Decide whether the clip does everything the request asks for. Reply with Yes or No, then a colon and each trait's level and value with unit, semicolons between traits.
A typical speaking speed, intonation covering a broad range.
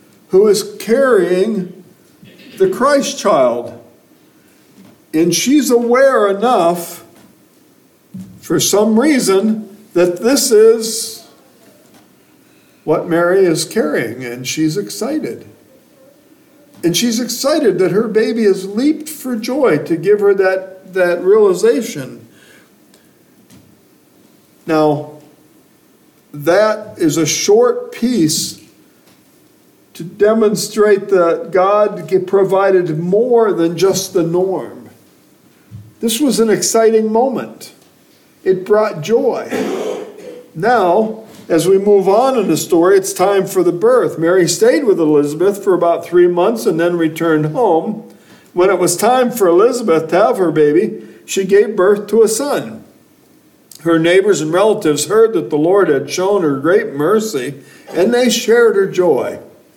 No: slow, 120 wpm; wide, 6.1 semitones